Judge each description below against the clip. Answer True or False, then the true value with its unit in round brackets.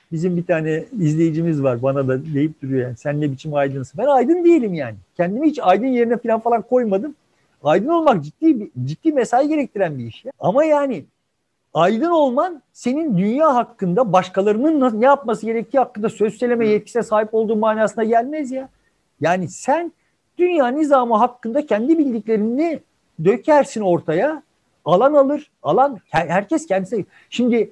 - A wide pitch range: True (7.5 semitones)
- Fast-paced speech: True (150 wpm)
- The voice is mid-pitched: False (225 Hz)